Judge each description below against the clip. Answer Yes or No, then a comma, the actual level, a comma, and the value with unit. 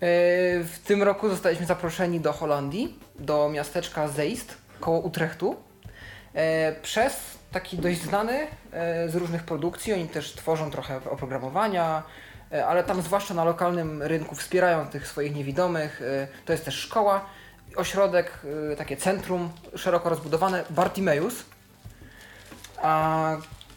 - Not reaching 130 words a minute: Yes, average, 115 wpm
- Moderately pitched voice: Yes, medium, 165 Hz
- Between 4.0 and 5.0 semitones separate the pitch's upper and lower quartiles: No, average, 3.3 semitones